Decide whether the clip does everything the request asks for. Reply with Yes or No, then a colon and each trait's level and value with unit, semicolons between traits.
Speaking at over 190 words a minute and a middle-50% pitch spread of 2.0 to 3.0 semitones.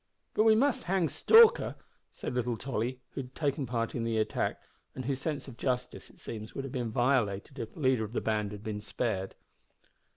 No: fast, 205 wpm; average, 4.0 semitones